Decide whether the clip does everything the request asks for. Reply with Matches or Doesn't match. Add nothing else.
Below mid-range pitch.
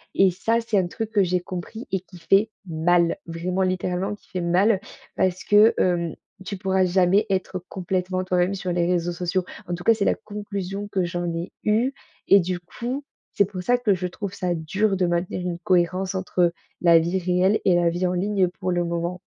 Doesn't match